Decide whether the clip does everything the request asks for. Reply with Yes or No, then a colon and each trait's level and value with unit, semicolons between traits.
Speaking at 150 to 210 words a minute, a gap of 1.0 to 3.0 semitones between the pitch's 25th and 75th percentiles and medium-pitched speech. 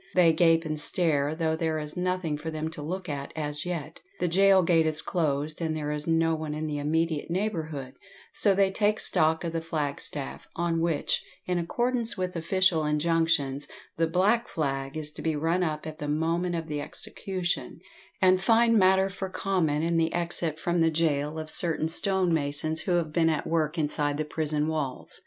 Yes: average, 190 wpm; average, 2.7 semitones; medium, 160 Hz